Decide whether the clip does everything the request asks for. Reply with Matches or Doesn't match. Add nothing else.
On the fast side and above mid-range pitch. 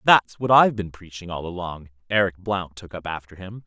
Doesn't match